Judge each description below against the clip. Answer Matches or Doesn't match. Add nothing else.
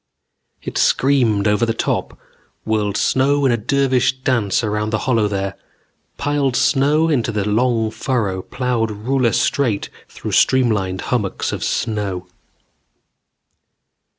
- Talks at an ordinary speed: Doesn't match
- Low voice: Matches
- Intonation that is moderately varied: Matches